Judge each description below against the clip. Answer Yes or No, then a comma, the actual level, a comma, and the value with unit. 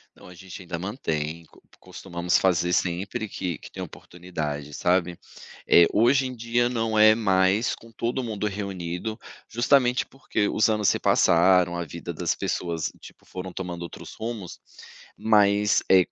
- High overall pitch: No, very low, 95 Hz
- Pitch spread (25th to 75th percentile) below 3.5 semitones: No, average, 4.1 semitones